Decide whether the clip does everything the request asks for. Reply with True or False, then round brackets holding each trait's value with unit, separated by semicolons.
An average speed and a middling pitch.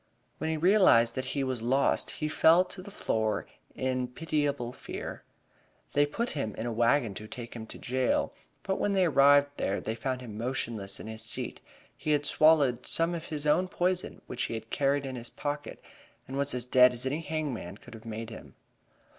False (195 wpm; 130 Hz)